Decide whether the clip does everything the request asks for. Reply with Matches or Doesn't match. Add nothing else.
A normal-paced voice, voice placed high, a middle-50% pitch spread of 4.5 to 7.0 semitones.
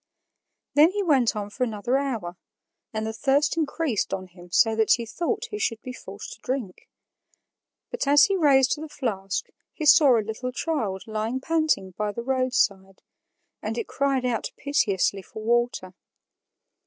Matches